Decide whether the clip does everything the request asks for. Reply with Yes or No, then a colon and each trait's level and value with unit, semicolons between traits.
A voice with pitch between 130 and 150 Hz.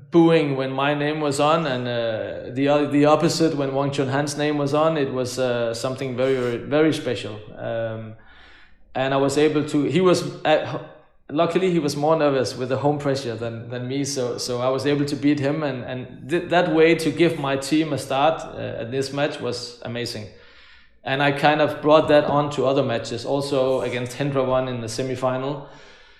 Yes: medium, 140 Hz